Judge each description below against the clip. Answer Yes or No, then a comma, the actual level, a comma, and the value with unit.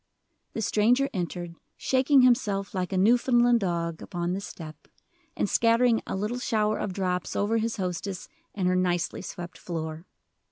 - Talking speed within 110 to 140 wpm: No, average, 155 wpm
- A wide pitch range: No, average, 4.5 semitones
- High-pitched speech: Yes, high, 195 Hz